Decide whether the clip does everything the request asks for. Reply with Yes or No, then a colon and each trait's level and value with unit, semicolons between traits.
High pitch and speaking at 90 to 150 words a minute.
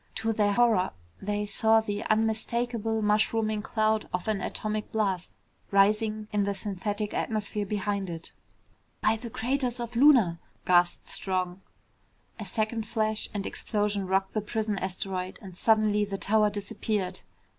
Yes: high, 210 Hz; average, 145 wpm